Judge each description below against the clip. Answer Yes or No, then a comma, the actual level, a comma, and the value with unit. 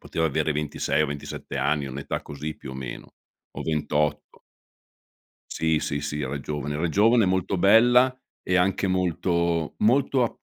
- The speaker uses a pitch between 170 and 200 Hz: No, very low, 80 Hz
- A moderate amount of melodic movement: Yes, average, 4.2 semitones